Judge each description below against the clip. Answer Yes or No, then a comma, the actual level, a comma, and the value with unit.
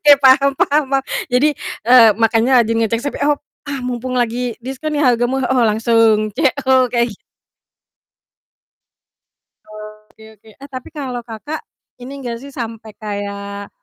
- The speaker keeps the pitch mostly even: No, average, 3.2 semitones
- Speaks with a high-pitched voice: Yes, high, 245 Hz